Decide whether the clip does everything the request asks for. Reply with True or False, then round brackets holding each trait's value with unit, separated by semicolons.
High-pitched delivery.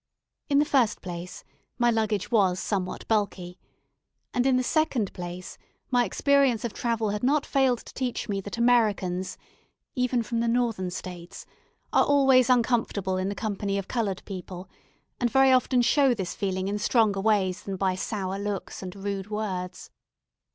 True (210 Hz)